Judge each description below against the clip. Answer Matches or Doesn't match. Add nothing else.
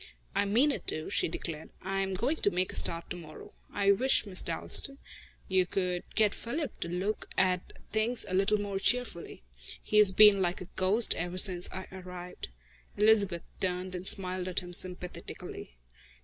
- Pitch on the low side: Doesn't match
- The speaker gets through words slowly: Doesn't match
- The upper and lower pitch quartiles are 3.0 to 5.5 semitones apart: Doesn't match